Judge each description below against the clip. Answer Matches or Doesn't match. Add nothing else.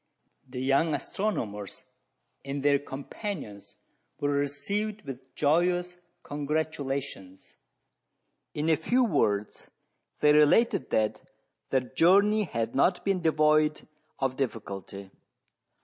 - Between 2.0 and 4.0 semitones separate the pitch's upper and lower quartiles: Doesn't match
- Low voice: Doesn't match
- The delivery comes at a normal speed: Doesn't match